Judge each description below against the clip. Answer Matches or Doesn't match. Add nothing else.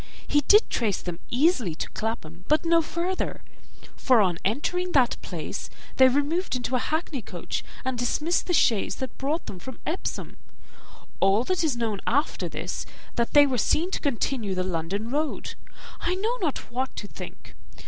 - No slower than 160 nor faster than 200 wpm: Matches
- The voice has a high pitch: Matches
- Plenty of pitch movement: Matches